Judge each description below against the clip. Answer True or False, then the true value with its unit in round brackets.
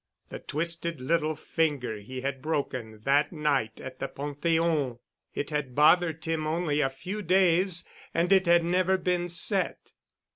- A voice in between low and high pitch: True (155 Hz)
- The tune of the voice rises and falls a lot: False (3.9 semitones)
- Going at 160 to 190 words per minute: False (150 wpm)